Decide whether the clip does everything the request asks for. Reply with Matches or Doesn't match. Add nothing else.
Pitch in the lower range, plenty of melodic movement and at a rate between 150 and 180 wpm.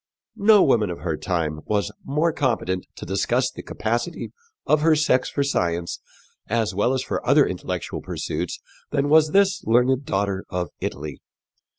Matches